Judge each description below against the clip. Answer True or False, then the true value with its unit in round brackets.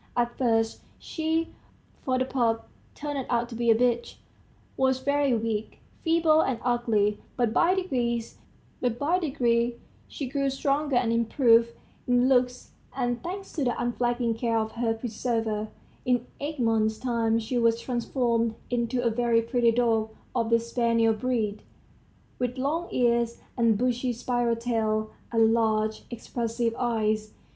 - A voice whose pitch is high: True (235 Hz)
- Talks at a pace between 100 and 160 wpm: True (140 wpm)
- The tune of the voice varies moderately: False (1.9 semitones)